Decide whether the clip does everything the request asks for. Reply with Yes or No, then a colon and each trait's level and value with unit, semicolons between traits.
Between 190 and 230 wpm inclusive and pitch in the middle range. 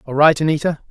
Yes: average, 200 wpm; medium, 150 Hz